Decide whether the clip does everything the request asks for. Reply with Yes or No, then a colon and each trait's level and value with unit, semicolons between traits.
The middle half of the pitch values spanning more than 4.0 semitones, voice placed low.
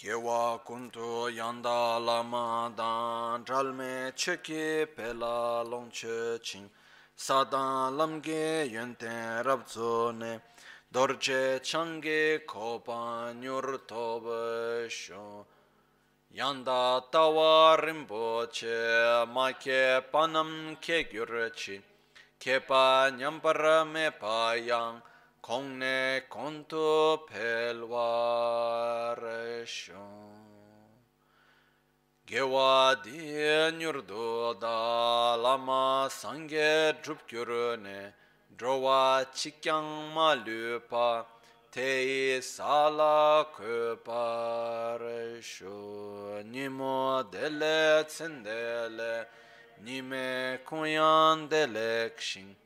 Yes: average, 4.4 semitones; low, 120 Hz